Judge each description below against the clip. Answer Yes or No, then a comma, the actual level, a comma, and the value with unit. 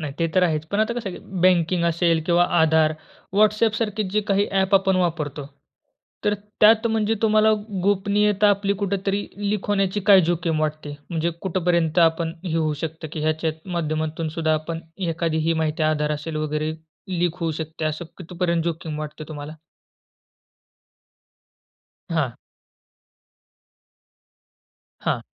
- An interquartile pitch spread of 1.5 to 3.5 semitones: No, average, 3.9 semitones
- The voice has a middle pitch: Yes, medium, 170 Hz